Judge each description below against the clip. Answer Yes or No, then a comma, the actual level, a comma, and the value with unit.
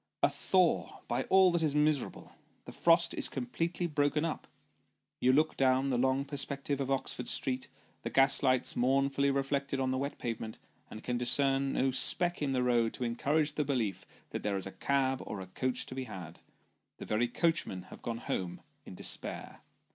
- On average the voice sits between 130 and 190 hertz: Yes, low, 135 Hz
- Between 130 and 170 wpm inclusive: No, average, 185 wpm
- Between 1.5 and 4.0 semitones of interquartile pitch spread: Yes, average, 2.8 semitones